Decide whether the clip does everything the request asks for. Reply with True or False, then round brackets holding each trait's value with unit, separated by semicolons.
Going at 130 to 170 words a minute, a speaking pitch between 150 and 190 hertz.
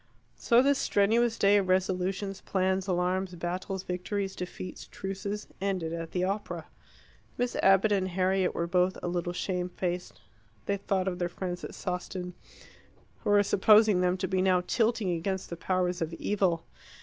True (160 wpm; 185 Hz)